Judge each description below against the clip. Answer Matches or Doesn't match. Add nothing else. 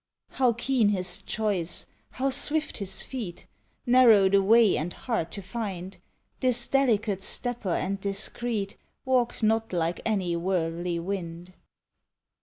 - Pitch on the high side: Matches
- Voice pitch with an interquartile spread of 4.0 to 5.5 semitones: Matches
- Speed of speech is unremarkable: Doesn't match